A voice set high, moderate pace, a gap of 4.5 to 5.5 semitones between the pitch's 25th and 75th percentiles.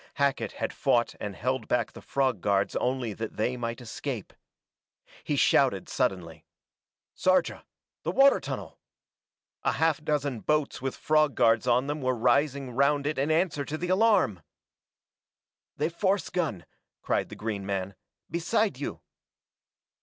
No: low, 135 Hz; average, 145 wpm; average, 5.1 semitones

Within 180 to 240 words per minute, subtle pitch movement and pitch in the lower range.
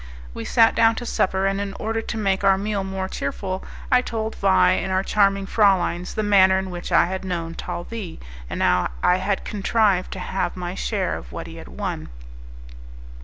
No: average, 195 wpm; narrow, 2.2 semitones; high, 190 Hz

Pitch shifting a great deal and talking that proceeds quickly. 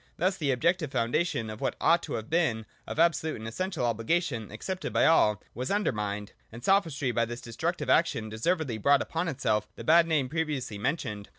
No: wide, 6.9 semitones; average, 190 wpm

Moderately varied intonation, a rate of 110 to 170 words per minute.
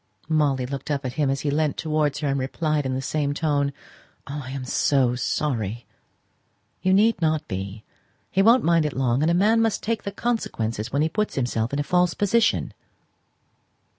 No: average, 4.5 semitones; average, 195 wpm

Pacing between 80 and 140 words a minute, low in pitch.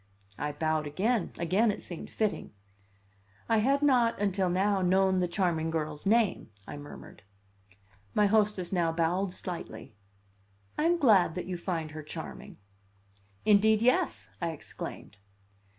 No: slow, 135 wpm; medium, 185 Hz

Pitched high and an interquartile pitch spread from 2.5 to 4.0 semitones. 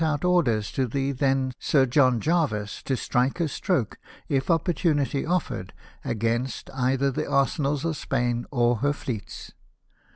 No: low, 135 Hz; average, 3.4 semitones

